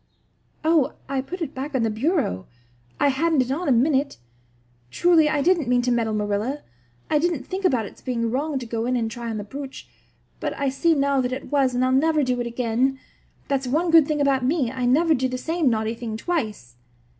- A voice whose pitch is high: Yes, very high, 265 Hz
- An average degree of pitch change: Yes, average, 4.0 semitones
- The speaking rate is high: Yes, fast, 220 wpm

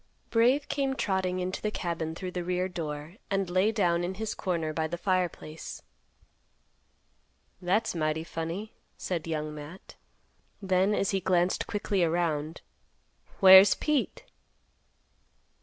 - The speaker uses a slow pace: Yes, slow, 125 wpm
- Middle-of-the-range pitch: Yes, medium, 180 Hz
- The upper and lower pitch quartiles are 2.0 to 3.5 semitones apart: Yes, average, 3.0 semitones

